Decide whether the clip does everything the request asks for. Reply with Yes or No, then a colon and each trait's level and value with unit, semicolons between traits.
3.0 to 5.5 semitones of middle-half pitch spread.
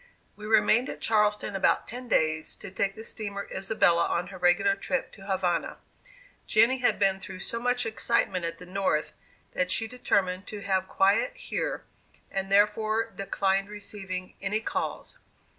No: narrow, 2.6 semitones